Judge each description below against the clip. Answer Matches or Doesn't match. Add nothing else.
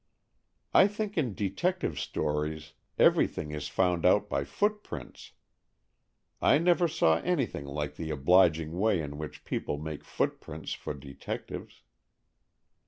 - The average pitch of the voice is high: Doesn't match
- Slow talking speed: Matches